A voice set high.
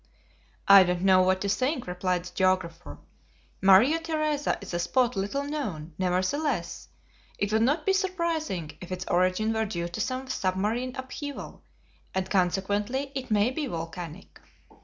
Yes: high, 200 Hz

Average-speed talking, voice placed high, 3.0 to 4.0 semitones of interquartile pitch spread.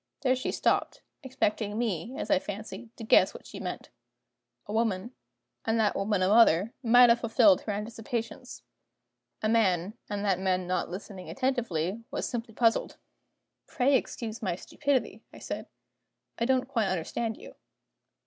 Yes: average, 155 wpm; high, 225 Hz; average, 3.5 semitones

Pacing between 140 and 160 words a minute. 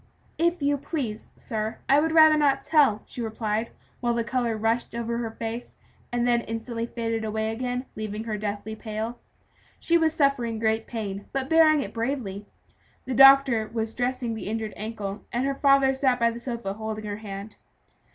No: average, 180 wpm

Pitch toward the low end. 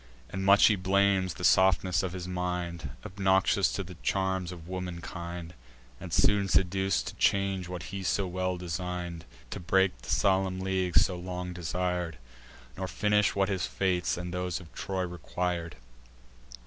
Yes: very low, 90 Hz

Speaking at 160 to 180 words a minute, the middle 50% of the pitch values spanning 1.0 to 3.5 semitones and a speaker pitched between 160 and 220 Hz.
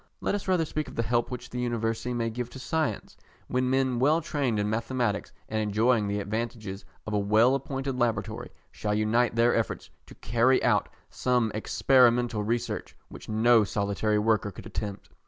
No: average, 175 wpm; average, 2.8 semitones; low, 115 Hz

